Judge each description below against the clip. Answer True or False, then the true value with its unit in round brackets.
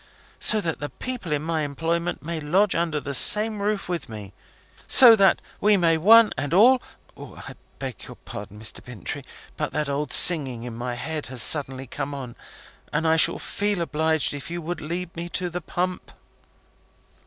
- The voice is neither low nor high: True (160 Hz)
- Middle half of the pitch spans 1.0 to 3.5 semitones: False (4.4 semitones)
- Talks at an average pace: True (180 wpm)